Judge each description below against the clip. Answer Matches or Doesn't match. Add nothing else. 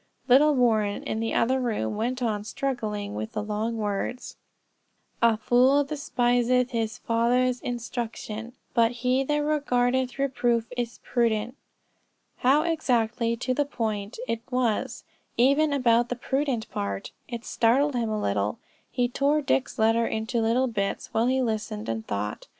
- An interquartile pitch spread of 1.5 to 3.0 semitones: Matches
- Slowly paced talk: Doesn't match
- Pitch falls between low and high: Doesn't match